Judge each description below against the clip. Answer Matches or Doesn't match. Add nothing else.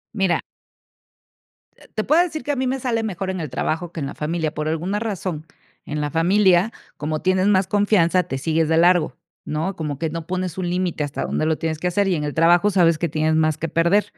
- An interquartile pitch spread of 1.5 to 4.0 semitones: Matches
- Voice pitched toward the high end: Doesn't match